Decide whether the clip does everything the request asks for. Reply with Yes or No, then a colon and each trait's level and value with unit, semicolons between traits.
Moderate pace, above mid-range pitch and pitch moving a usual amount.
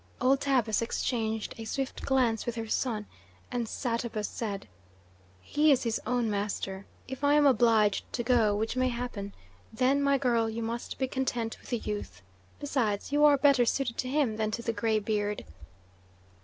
Yes: average, 170 wpm; high, 235 Hz; average, 3.2 semitones